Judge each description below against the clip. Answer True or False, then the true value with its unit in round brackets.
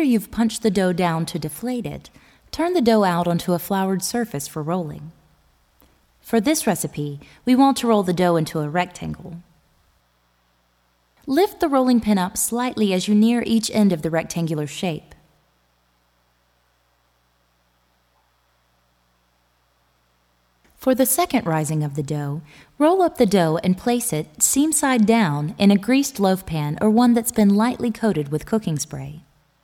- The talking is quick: False (155 wpm)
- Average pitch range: False (8.4 semitones)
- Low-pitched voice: False (175 Hz)